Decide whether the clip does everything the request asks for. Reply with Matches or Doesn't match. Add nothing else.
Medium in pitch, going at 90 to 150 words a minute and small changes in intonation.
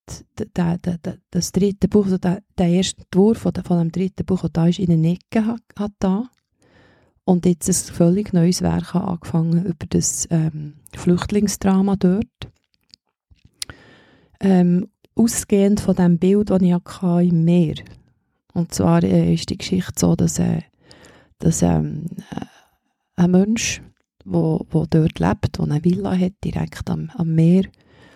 Matches